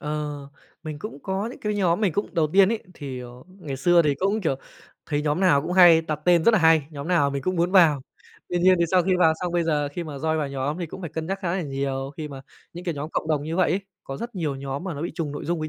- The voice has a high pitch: No, medium, 160 Hz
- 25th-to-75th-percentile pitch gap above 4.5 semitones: No, average, 3.8 semitones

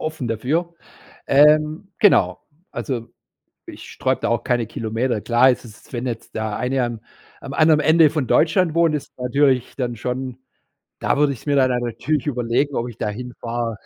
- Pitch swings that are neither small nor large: Yes, average, 4.3 semitones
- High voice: No, low, 130 Hz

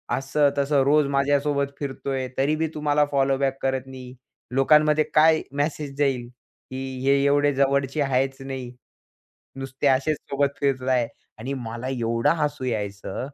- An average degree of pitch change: No, narrow, 1.7 semitones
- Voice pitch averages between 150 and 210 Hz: No, low, 135 Hz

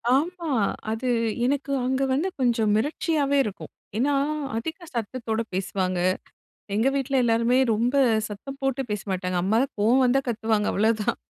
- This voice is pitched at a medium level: No, high, 240 Hz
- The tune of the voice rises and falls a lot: No, average, 4.3 semitones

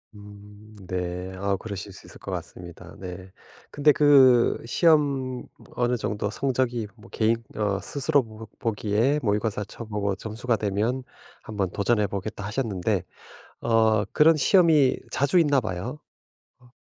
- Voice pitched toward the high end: No, low, 110 Hz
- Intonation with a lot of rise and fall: No, average, 4.3 semitones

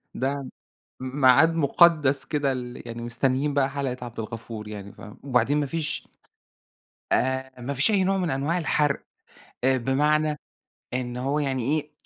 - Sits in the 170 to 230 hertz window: No, low, 135 Hz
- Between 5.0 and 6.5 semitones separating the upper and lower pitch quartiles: No, average, 2.9 semitones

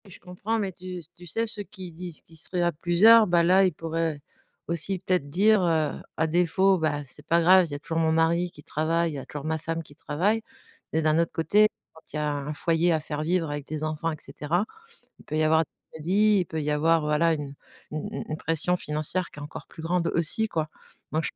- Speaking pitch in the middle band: Yes, medium, 165 Hz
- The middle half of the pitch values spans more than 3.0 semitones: No, average, 2.7 semitones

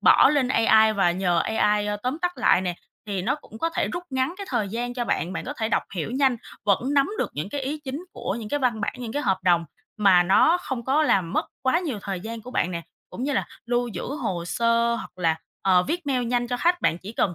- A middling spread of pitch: No, wide, 5.7 semitones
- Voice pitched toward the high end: Yes, high, 235 Hz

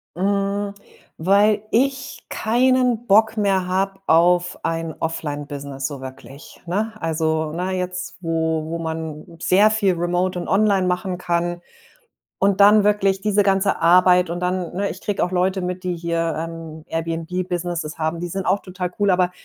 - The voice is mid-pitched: Yes, medium, 180 Hz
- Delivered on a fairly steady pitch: No, average, 3.1 semitones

